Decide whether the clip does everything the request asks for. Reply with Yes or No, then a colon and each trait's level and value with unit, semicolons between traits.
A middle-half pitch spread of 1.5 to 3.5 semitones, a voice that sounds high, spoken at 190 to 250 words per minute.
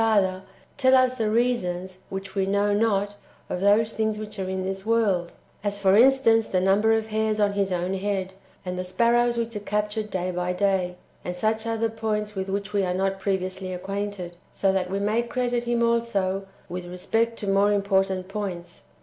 Yes: average, 2.8 semitones; high, 200 Hz; average, 200 wpm